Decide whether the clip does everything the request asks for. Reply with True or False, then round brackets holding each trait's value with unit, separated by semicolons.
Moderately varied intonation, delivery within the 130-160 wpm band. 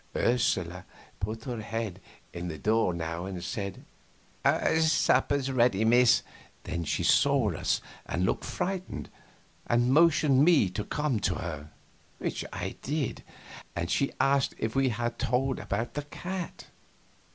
False (6.7 semitones; 140 wpm)